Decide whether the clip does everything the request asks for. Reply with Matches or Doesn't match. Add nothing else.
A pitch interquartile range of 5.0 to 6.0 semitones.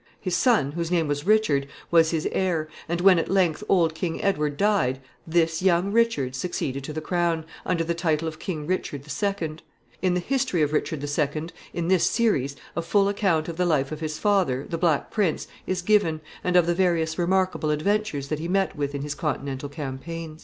Doesn't match